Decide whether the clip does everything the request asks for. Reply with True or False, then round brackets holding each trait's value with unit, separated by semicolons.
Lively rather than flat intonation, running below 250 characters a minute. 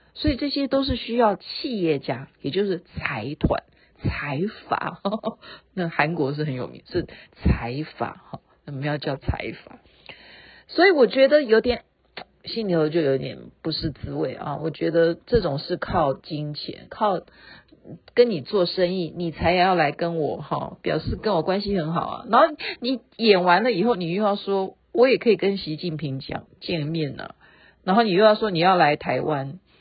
True (6.1 semitones; 240 characters per minute)